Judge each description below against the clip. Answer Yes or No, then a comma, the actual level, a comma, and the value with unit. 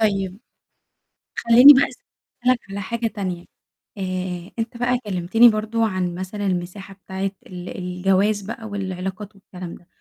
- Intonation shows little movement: No, average, 3.2 semitones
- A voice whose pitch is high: Yes, high, 195 Hz